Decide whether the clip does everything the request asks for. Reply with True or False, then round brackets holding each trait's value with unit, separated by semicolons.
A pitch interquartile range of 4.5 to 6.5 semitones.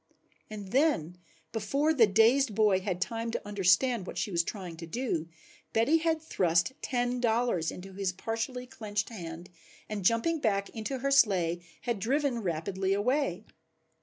True (5.0 semitones)